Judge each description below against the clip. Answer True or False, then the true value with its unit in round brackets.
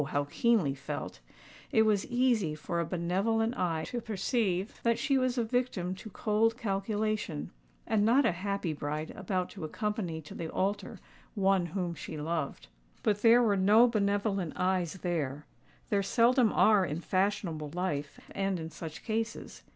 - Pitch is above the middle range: True (195 Hz)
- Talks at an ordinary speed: True (150 wpm)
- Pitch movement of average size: True (4.6 semitones)